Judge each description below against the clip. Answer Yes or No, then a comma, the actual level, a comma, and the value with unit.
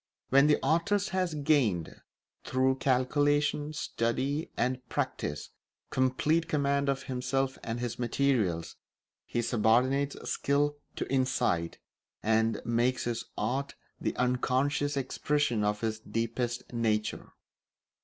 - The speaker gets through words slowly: Yes, slow, 110 wpm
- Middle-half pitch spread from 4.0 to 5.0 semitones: No, average, 3.5 semitones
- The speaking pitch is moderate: No, low, 130 Hz